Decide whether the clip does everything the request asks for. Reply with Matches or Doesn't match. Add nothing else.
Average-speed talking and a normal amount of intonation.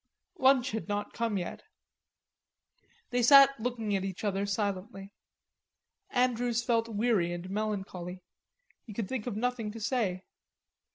Doesn't match